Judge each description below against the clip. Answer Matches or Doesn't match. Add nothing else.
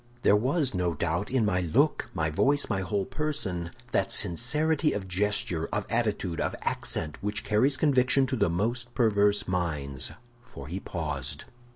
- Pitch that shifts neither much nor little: Doesn't match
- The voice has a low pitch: Matches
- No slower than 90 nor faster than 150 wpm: Doesn't match